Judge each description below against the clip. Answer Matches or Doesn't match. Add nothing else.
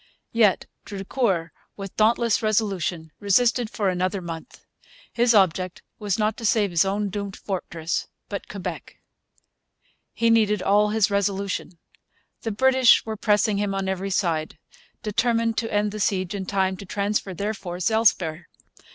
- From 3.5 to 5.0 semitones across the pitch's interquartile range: Doesn't match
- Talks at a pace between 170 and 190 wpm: Doesn't match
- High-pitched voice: Matches